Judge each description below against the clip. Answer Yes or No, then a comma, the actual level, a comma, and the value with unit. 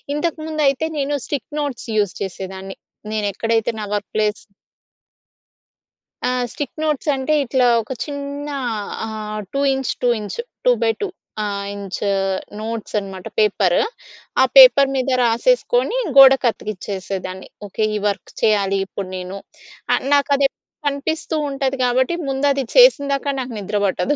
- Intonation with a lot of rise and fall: Yes, wide, 5.7 semitones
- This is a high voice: Yes, high, 245 Hz